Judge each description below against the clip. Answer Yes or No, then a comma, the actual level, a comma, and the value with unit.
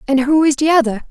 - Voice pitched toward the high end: Yes, very high, 280 Hz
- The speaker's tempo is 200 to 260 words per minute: No, fast, 270 wpm